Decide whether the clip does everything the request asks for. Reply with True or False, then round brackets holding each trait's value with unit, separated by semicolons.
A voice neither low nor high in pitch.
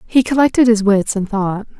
False (220 Hz)